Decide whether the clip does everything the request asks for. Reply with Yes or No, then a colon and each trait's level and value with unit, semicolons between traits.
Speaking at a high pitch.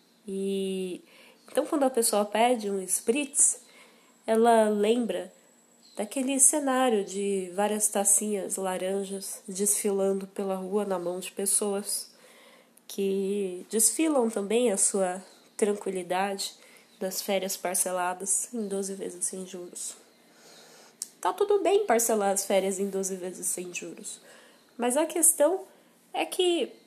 Yes: high, 205 Hz